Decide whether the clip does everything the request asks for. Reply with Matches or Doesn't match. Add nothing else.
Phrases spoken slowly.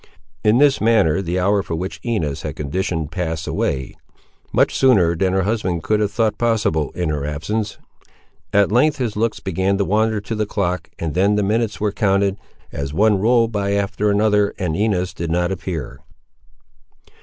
Doesn't match